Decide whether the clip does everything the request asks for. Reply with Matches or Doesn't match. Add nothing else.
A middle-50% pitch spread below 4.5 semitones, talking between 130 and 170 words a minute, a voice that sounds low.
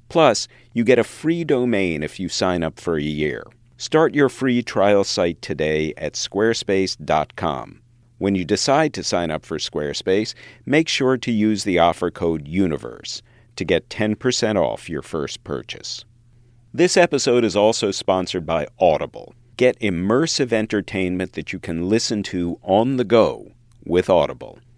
Doesn't match